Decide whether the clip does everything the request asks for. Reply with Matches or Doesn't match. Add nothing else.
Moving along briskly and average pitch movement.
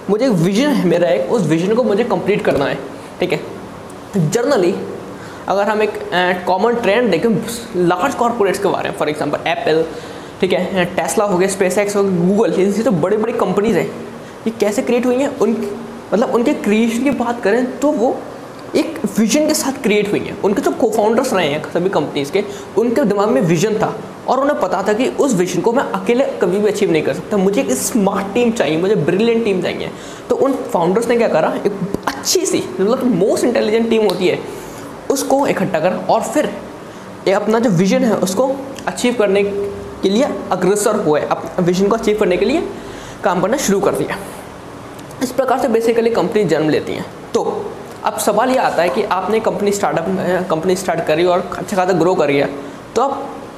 Matches